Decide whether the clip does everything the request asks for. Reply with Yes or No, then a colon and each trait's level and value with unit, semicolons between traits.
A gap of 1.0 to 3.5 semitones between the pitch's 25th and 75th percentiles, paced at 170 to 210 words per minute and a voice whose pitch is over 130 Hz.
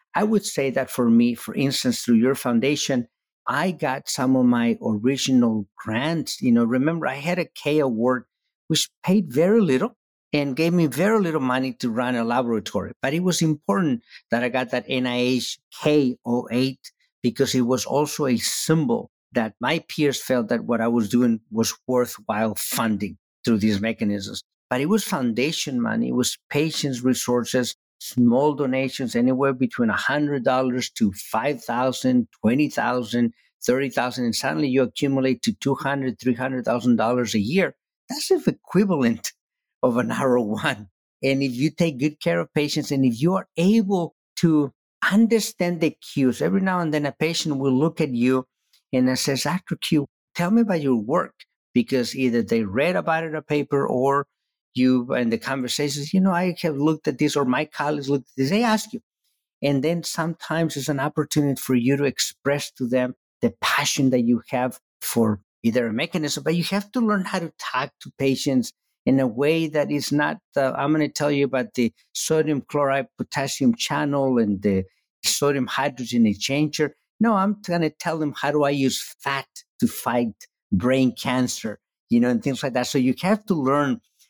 No: average, 4.3 semitones; average, 180 wpm; medium, 140 Hz